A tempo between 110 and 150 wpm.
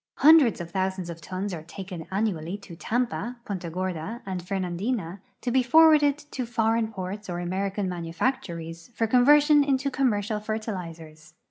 Yes: average, 145 wpm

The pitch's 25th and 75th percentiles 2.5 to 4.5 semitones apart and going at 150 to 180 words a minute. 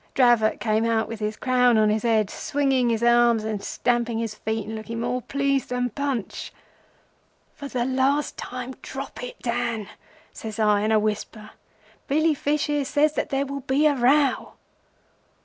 Yes: average, 3.7 semitones; average, 170 wpm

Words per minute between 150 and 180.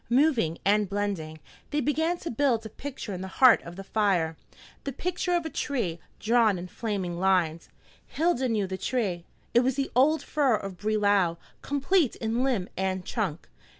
Yes: average, 175 wpm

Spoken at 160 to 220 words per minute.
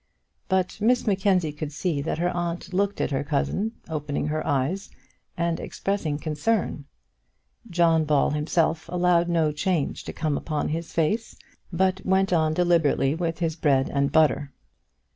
No: average, 150 wpm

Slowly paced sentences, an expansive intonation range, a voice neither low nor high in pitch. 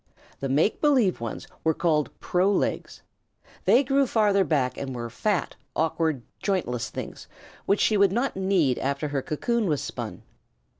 No: average, 155 wpm; wide, 6.7 semitones; medium, 170 Hz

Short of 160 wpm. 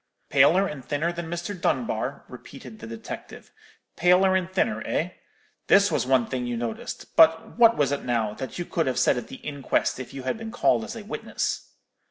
No: average, 200 wpm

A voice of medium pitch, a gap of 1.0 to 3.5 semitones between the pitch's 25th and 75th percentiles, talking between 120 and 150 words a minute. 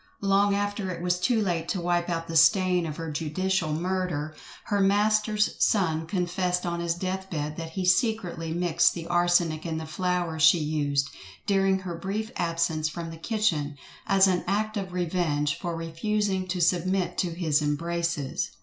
No: medium, 175 Hz; average, 2.7 semitones; average, 170 wpm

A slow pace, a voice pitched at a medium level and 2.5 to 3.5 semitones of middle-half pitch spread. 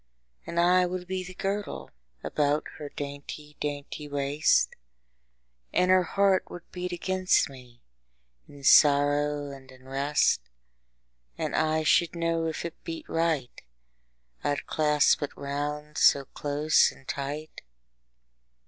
Yes: slow, 130 wpm; medium, 150 Hz; average, 3.0 semitones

